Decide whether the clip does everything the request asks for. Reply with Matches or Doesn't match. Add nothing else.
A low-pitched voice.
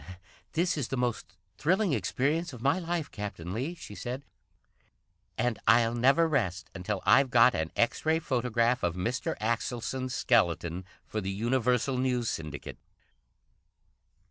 Matches